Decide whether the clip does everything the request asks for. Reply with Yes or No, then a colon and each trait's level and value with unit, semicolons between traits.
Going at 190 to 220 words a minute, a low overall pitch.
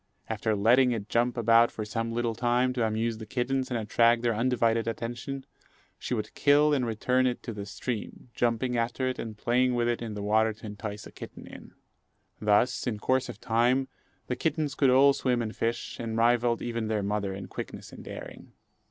Yes: average, 200 wpm; low, 115 Hz